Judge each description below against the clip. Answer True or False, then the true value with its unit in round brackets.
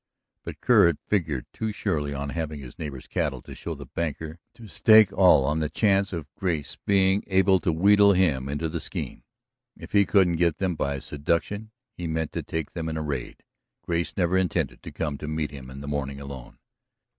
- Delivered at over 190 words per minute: True (205 wpm)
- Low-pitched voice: True (80 Hz)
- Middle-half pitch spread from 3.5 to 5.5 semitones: True (4.6 semitones)